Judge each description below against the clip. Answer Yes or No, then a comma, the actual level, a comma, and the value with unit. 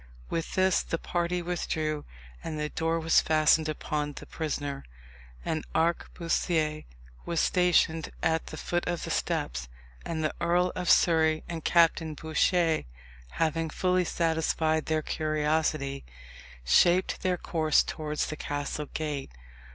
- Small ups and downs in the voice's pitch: Yes, narrow, 1.8 semitones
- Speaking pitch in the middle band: Yes, medium, 160 Hz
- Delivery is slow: Yes, slow, 130 wpm